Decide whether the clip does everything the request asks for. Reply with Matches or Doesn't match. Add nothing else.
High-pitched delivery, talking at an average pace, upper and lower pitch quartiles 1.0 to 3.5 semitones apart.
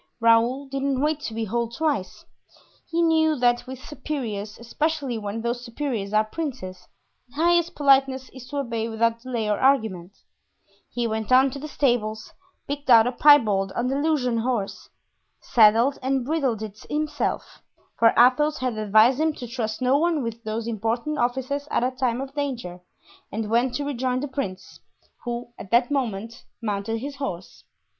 Doesn't match